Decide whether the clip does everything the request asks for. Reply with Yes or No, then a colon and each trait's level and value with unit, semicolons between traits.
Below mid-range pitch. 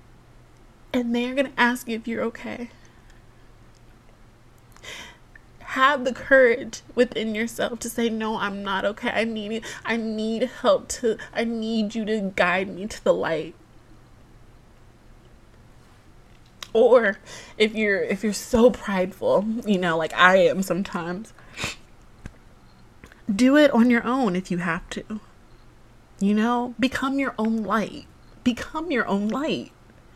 No: high, 220 Hz